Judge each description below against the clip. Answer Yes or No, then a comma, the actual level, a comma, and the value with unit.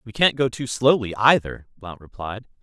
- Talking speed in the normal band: Yes, average, 185 wpm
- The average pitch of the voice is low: Yes, low, 115 Hz